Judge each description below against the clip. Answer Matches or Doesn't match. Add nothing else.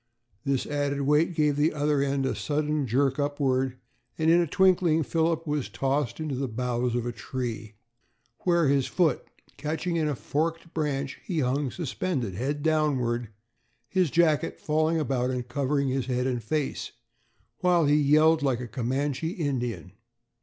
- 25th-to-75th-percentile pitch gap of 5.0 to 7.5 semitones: Doesn't match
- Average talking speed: Matches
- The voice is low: Doesn't match